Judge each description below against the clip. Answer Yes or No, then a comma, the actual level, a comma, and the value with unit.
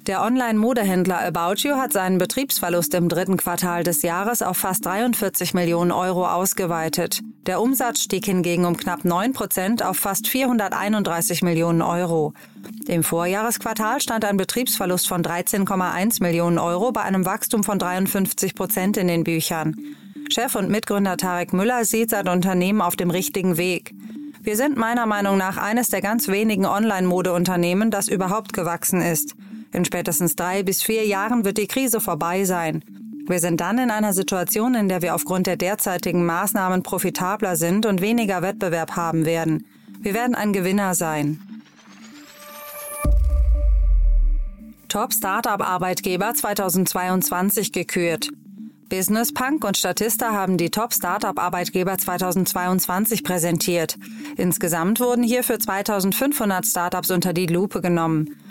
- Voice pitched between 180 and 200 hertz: Yes, high, 190 Hz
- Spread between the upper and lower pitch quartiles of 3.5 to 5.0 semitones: Yes, average, 3.8 semitones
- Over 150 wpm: No, average, 140 wpm